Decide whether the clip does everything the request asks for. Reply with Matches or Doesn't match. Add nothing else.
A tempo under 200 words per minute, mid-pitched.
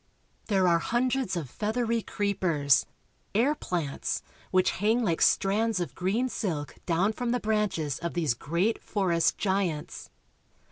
Doesn't match